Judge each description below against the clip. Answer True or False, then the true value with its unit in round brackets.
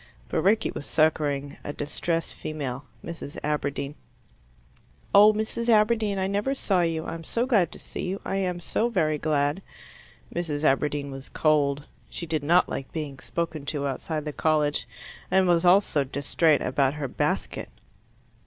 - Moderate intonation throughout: True (4.4 semitones)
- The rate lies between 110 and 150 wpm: False (160 wpm)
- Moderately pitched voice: True (155 Hz)